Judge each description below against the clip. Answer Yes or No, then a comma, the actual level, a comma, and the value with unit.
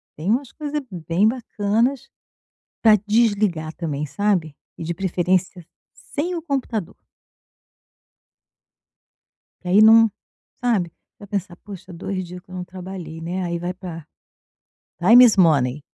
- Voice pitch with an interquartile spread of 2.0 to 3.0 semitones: No, average, 4.3 semitones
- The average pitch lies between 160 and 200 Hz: Yes, high, 190 Hz